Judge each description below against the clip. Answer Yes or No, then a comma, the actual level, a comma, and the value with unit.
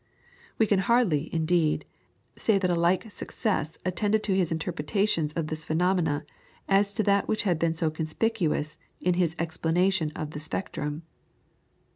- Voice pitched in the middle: Yes, medium, 170 Hz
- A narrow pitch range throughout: No, average, 3.8 semitones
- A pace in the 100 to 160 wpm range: Yes, average, 140 wpm